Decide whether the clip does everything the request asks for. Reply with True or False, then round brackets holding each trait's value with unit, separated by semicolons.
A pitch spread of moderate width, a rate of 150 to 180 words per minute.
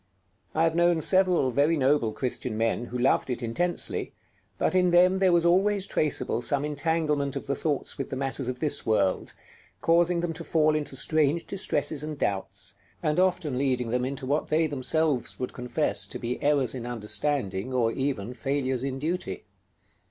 True (4.5 semitones; 175 wpm)